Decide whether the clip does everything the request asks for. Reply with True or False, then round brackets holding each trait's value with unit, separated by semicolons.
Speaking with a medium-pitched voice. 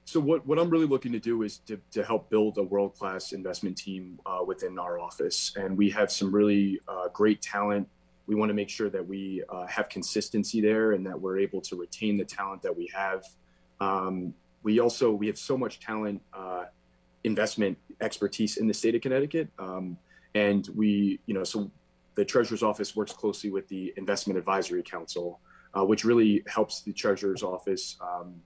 False (100 Hz)